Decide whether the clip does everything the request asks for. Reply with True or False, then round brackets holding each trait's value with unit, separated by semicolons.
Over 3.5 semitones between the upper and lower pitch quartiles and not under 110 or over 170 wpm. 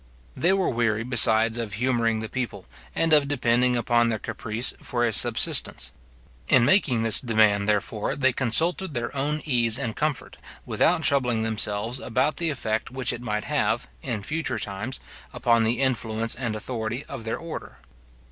False (3.0 semitones; 165 wpm)